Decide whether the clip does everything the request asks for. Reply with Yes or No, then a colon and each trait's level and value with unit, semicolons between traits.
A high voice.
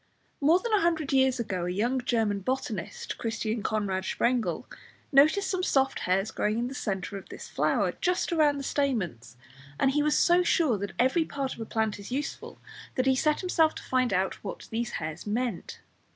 Yes: very high, 250 Hz